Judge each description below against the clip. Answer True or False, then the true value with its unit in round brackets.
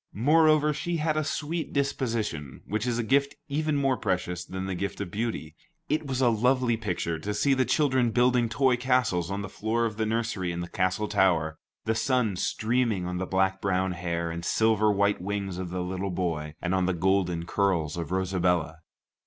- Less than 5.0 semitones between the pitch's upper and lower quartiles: False (5.6 semitones)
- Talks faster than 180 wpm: True (195 wpm)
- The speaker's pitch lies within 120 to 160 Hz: False (100 Hz)